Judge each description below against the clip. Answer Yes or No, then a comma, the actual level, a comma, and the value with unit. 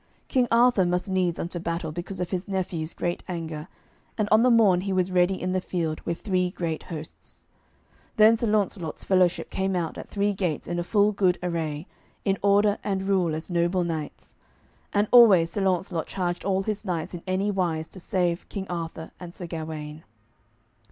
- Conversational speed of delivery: Yes, average, 185 wpm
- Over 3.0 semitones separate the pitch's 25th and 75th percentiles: No, average, 2.7 semitones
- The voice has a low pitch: No, medium, 180 Hz